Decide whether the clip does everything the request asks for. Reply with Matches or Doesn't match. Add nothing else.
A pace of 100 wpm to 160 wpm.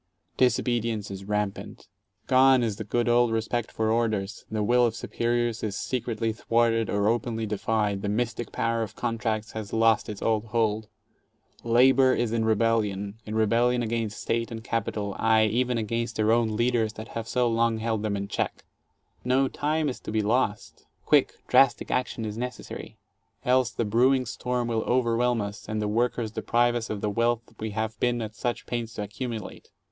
Doesn't match